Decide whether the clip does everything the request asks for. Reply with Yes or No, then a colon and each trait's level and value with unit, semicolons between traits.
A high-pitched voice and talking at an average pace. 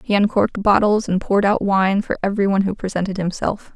No: high, 200 Hz; fast, 210 wpm